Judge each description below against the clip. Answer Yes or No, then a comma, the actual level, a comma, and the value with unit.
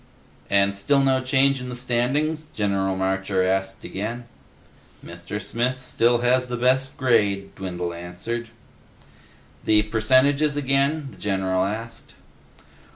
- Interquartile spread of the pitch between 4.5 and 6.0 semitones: Yes, average, 5.2 semitones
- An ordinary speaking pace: No, slow, 120 wpm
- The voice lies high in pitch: No, low, 115 Hz